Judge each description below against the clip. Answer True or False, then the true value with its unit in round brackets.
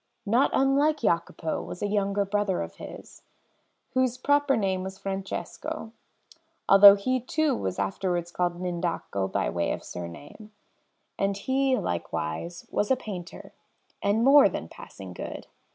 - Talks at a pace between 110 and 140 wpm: True (135 wpm)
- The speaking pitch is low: False (195 Hz)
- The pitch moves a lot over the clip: True (6.7 semitones)